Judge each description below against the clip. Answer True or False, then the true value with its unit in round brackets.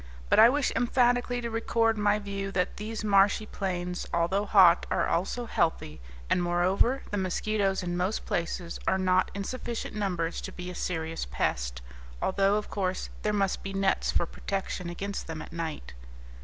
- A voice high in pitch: True (195 Hz)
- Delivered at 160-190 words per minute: True (170 wpm)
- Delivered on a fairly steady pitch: False (3.2 semitones)